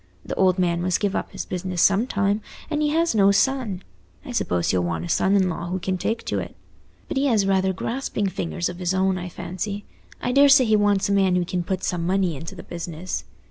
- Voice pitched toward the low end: No, high, 190 Hz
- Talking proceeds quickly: Yes, fast, 230 wpm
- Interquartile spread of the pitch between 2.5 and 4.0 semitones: Yes, average, 2.8 semitones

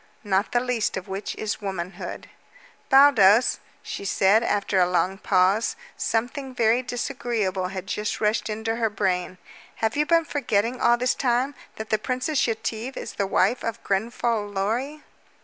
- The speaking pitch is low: No, high, 220 Hz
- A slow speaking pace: No, average, 155 wpm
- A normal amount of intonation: Yes, average, 3.9 semitones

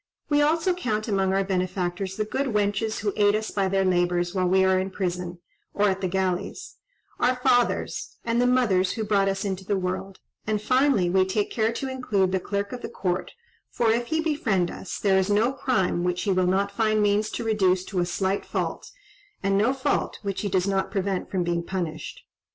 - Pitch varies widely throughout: No, average, 2.8 semitones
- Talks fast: Yes, fast, 210 wpm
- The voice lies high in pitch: Yes, high, 195 Hz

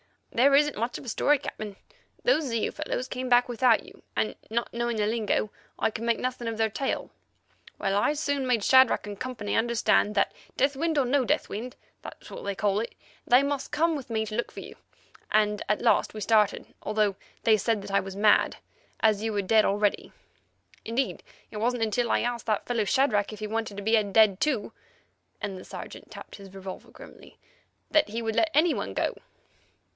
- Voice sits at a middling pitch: No, high, 225 Hz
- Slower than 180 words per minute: No, average, 195 wpm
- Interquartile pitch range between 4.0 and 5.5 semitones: No, average, 3.3 semitones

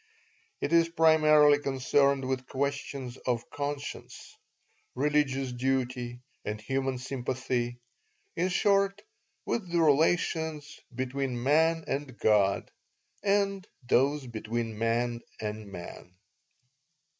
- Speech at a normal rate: No, slow, 100 wpm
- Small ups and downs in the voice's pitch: No, average, 3.9 semitones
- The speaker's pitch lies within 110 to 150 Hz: Yes, low, 135 Hz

